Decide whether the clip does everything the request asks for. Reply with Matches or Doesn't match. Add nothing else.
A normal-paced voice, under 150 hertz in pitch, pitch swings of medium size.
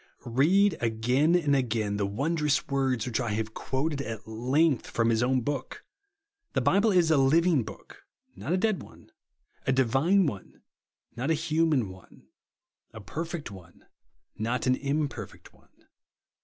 Doesn't match